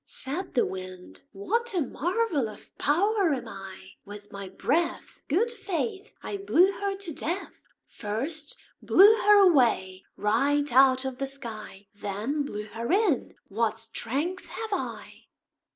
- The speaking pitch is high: Yes, very high, 280 Hz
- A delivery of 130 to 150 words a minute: Yes, average, 140 wpm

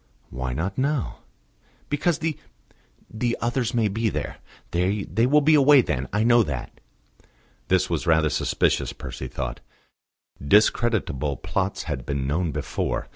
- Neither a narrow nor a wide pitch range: No, wide, 7.8 semitones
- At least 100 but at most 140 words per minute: Yes, slow, 135 wpm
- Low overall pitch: Yes, low, 100 Hz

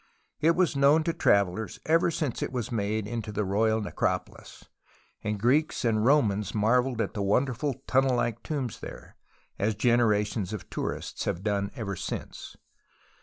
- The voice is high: No, low, 115 Hz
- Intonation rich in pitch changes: No, average, 4.3 semitones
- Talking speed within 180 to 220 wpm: No, average, 155 wpm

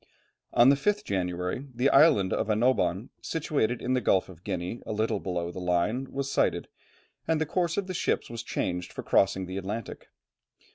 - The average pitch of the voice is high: No, low, 110 Hz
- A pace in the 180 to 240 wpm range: Yes, average, 185 wpm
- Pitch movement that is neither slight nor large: No, wide, 6.8 semitones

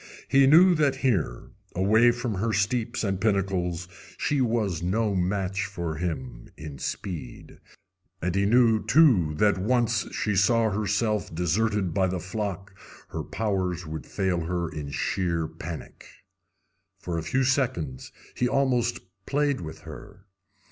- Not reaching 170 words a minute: Yes, average, 140 wpm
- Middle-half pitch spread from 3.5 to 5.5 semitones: Yes, average, 4.8 semitones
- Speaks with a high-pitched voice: No, low, 100 Hz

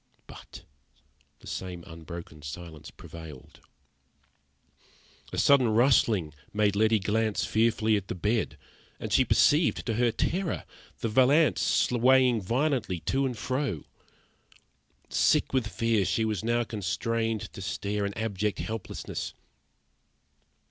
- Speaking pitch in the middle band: No, low, 110 Hz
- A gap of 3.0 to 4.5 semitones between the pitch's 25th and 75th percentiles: Yes, average, 3.8 semitones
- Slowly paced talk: Yes, slow, 120 wpm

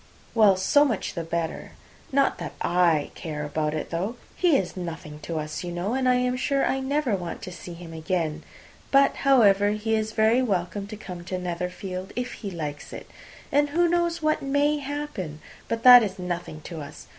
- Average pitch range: No, wide, 7.2 semitones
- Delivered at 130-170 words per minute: No, average, 195 wpm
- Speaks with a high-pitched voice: Yes, high, 195 Hz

